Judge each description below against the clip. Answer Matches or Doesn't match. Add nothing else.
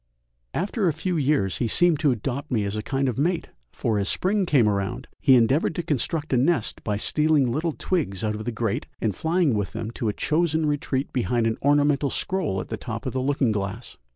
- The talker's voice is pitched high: Doesn't match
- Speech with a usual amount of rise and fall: Doesn't match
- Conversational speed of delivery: Doesn't match